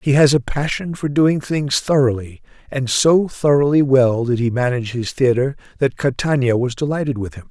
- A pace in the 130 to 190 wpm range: Yes, average, 185 wpm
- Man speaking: Yes, male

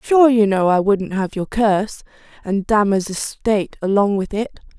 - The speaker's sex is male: No, female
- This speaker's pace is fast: No, average, 175 wpm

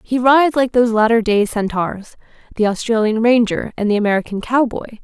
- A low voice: No, high, 225 Hz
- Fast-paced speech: No, average, 155 wpm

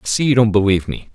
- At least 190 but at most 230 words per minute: No, fast, 315 wpm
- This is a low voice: Yes, low, 105 Hz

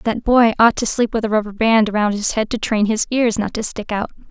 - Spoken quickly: Yes, fast, 280 wpm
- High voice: Yes, high, 220 Hz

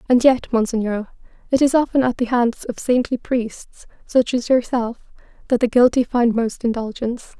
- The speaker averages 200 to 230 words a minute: No, average, 170 wpm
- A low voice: No, high, 240 Hz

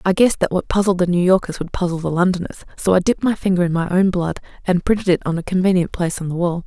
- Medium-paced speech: No, fast, 280 wpm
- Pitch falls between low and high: Yes, medium, 180 Hz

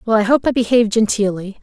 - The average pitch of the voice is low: No, high, 220 Hz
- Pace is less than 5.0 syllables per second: No, 6.8 syllables/s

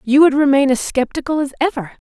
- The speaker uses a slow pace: No, average, 200 wpm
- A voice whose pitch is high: Yes, very high, 280 Hz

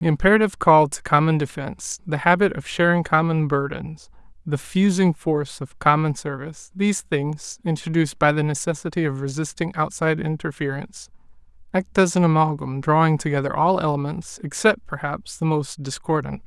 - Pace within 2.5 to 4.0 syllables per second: No, 5.4 syllables/s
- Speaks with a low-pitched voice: No, medium, 160 Hz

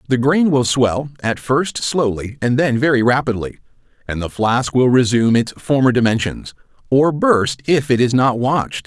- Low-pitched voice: Yes, low, 125 Hz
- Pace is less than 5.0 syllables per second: Yes, 4.7 syllables/s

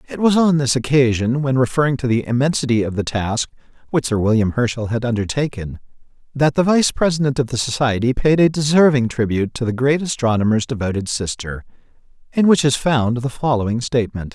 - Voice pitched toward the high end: No, low, 125 Hz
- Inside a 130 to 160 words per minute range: No, average, 180 wpm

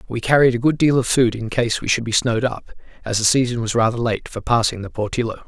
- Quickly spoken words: Yes, fast, 265 wpm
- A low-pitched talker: Yes, low, 115 Hz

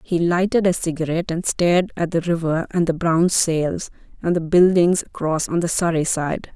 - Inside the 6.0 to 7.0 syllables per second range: No, 4.9 syllables/s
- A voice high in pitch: No, medium, 170 Hz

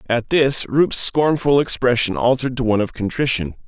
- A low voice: Yes, low, 125 Hz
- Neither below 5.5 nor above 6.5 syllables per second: Yes, 5.6 syllables/s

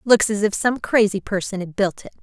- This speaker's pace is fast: Yes, fast, 240 wpm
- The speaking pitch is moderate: No, high, 205 Hz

